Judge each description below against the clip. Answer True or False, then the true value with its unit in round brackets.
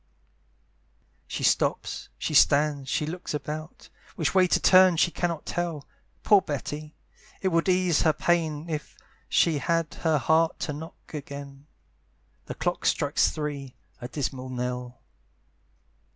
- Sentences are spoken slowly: True (130 wpm)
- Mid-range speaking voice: True (155 Hz)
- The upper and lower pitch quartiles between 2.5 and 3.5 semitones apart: True (2.9 semitones)